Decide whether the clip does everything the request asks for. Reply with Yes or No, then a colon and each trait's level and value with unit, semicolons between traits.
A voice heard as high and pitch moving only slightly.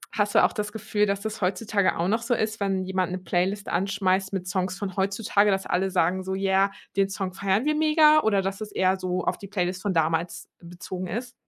Yes: high, 195 Hz; narrow, 2.0 semitones